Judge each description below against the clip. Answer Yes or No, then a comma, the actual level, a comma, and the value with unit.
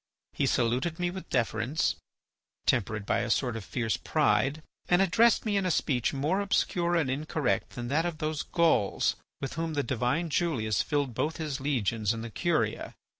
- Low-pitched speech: No, medium, 145 Hz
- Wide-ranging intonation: Yes, wide, 5.9 semitones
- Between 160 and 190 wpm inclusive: Yes, average, 175 wpm